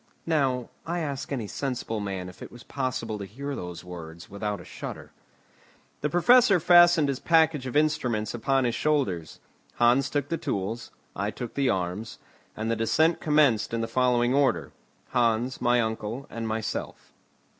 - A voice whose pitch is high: No, low, 120 Hz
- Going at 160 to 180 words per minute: Yes, average, 165 wpm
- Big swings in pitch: No, average, 4.8 semitones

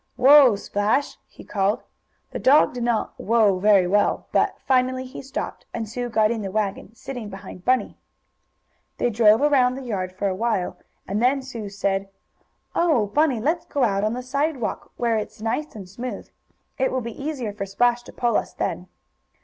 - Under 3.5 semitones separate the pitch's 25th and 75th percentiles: No, average, 3.9 semitones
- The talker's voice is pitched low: No, high, 230 Hz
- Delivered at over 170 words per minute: Yes, average, 180 wpm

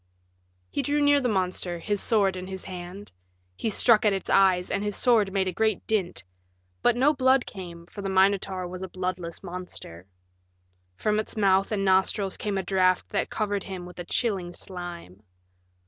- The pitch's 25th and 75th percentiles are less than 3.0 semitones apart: Yes, narrow, 2.6 semitones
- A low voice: No, high, 190 Hz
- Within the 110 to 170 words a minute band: No, average, 180 wpm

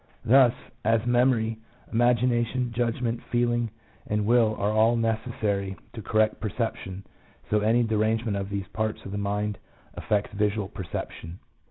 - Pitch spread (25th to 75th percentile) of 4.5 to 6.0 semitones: No, narrow, 2.4 semitones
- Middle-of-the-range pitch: No, low, 110 Hz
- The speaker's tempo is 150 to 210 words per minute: No, average, 140 wpm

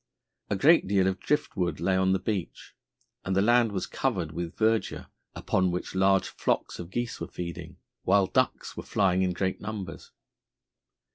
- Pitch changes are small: Yes, narrow, 2.3 semitones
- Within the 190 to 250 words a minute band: No, average, 170 wpm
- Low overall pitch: Yes, very low, 95 Hz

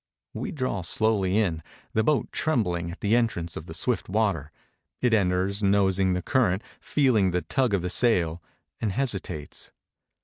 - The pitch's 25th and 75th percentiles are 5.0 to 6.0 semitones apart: No, average, 4.1 semitones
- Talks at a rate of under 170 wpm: Yes, average, 160 wpm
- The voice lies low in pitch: Yes, low, 100 Hz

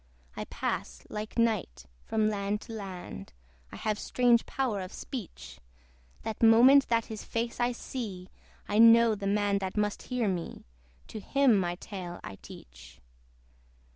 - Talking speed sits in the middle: Yes, average, 150 wpm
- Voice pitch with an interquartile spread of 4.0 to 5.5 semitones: No, average, 3.5 semitones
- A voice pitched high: Yes, high, 210 Hz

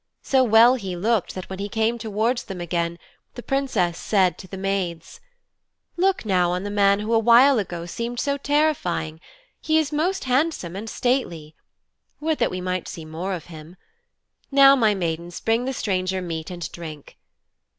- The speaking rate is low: No, average, 175 wpm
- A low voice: No, high, 200 Hz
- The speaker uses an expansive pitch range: Yes, wide, 6.2 semitones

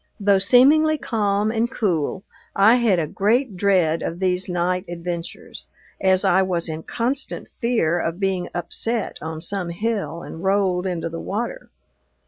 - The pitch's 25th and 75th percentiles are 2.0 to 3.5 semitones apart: No, average, 4.3 semitones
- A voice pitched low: No, high, 190 Hz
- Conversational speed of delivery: Yes, average, 150 wpm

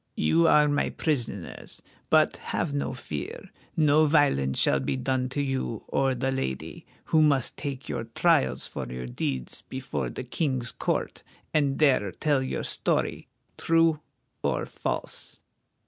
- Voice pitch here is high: No, low, 130 Hz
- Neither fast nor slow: Yes, average, 145 wpm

